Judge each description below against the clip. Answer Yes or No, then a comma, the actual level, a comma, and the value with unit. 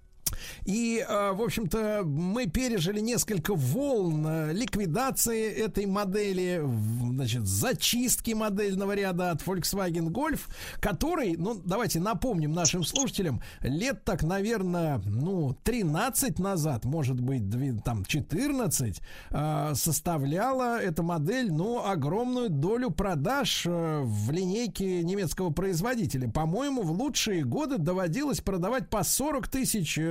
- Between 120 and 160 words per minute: No, slow, 110 wpm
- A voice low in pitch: No, medium, 185 Hz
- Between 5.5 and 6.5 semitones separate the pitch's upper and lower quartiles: Yes, wide, 6.0 semitones